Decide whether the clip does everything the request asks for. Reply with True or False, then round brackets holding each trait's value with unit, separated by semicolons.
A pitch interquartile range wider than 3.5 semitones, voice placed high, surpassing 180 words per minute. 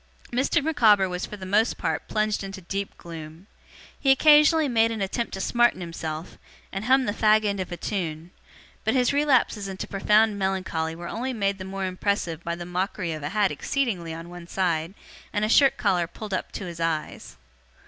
True (4.3 semitones; 195 Hz; 195 wpm)